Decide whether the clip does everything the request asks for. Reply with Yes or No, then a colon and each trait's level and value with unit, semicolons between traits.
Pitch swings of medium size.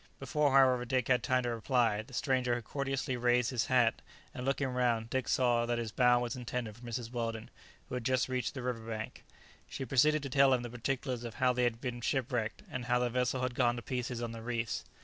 No: narrow, 1.5 semitones